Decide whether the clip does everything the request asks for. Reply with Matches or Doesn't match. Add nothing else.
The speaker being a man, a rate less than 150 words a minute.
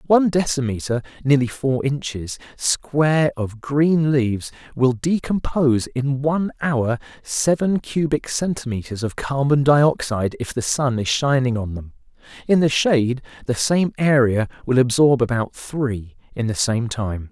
Matches